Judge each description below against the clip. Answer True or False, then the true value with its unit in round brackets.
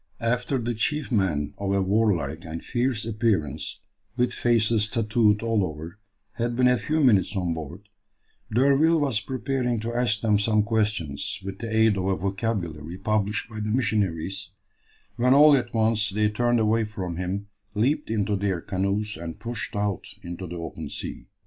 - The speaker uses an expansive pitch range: False (3.6 semitones)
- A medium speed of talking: True (170 wpm)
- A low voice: True (105 Hz)